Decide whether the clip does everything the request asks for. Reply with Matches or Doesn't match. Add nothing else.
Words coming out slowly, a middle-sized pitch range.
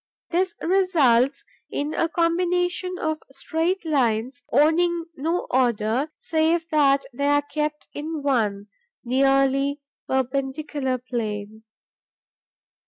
Matches